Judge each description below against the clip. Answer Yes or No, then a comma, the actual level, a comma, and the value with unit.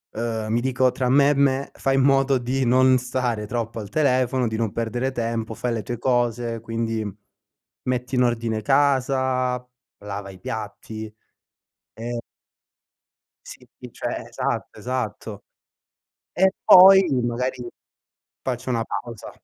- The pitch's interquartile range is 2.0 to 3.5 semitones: Yes, narrow, 2.4 semitones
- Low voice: Yes, low, 120 Hz